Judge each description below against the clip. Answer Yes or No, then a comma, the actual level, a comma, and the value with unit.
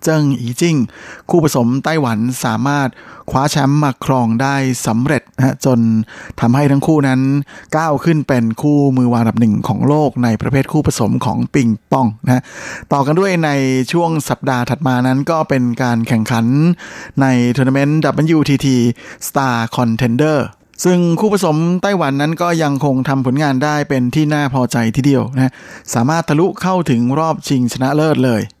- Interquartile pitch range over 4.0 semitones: No, average, 3.6 semitones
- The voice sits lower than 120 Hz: No, low, 135 Hz